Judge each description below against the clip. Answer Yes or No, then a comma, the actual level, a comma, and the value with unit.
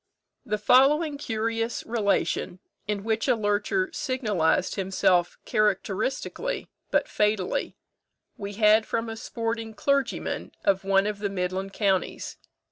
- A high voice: Yes, high, 215 Hz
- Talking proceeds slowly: Yes, slow, 120 wpm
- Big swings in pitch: No, narrow, 2.6 semitones